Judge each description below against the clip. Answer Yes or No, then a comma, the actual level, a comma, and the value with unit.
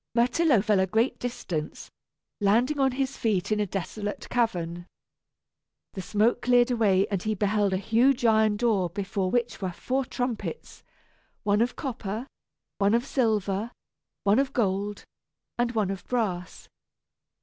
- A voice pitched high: Yes, high, 215 Hz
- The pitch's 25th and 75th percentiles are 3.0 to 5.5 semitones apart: Yes, average, 3.6 semitones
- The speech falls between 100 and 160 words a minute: Yes, average, 145 wpm